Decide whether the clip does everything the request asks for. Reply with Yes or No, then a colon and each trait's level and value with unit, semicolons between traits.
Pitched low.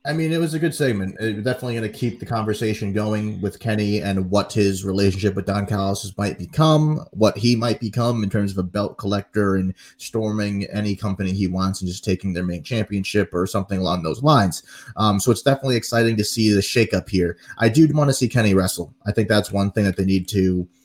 Yes: low, 105 Hz